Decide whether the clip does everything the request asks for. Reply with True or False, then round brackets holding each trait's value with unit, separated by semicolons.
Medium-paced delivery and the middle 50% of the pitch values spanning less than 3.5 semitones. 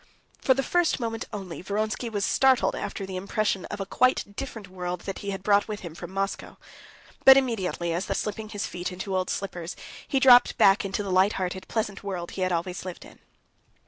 False (210 wpm; 2.9 semitones)